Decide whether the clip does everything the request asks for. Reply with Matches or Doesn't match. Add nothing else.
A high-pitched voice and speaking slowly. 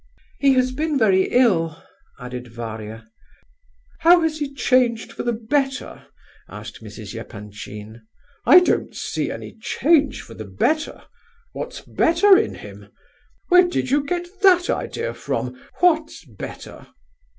Matches